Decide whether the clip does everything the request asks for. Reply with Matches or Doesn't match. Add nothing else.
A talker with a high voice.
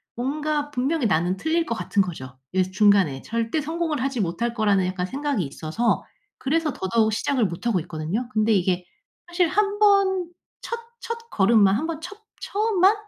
Matches